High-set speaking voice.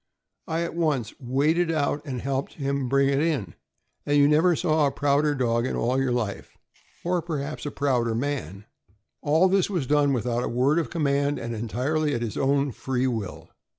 No: medium, 140 Hz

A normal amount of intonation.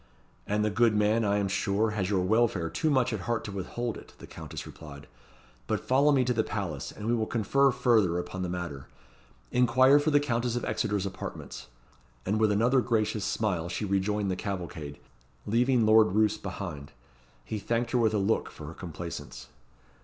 Yes: average, 4.0 semitones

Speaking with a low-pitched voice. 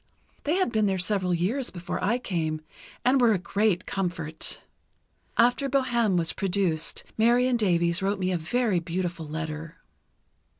No: high, 190 Hz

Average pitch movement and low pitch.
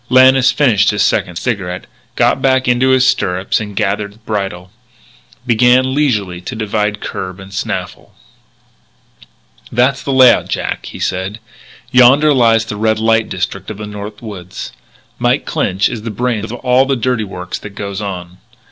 Yes: average, 4.2 semitones; low, 110 Hz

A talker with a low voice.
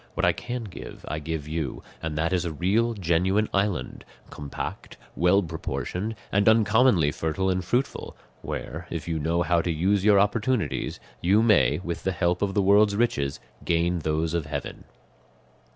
Yes: very low, 90 Hz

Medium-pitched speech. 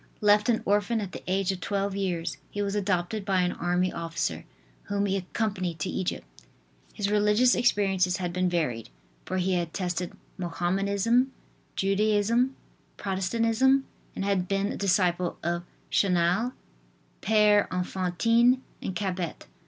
No: high, 195 Hz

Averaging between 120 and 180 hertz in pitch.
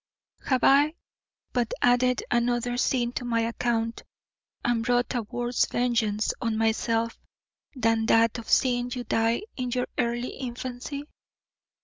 No: high, 240 Hz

